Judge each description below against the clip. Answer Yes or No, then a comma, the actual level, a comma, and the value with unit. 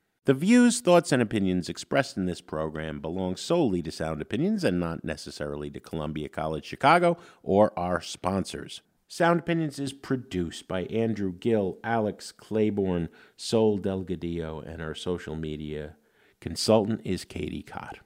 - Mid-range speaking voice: No, very low, 90 Hz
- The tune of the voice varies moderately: No, wide, 6.1 semitones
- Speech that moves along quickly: No, average, 145 wpm